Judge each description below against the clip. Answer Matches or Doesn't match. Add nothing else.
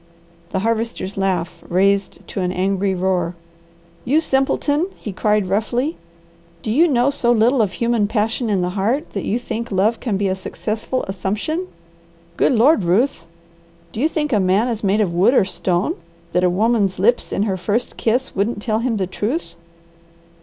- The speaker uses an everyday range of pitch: Matches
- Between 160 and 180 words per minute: Matches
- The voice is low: Doesn't match